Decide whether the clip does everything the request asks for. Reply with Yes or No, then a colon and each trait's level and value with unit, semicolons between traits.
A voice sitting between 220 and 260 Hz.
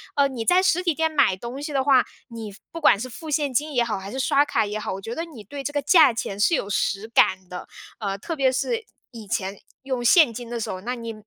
Yes: high, 245 Hz